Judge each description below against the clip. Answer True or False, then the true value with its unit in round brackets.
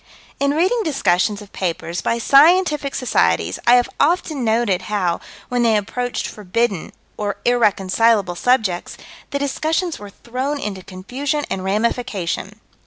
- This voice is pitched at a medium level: False (230 Hz)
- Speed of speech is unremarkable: False (130 wpm)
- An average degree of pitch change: False (6.2 semitones)